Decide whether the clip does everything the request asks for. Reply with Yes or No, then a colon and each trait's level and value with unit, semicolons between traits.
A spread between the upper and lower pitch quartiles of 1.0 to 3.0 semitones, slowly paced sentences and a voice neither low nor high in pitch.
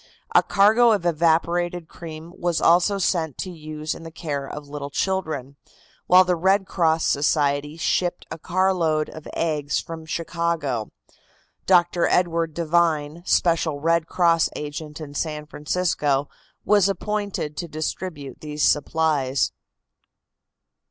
Yes: average, 2.7 semitones; slow, 125 wpm; medium, 165 Hz